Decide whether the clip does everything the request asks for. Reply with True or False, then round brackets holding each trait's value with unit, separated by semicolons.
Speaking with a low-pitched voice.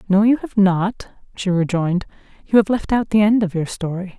False (195 Hz)